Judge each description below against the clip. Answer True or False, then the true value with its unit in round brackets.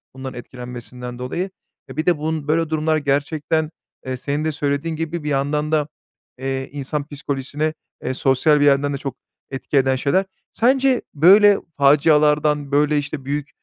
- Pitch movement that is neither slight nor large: False (2.3 semitones)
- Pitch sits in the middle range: True (145 Hz)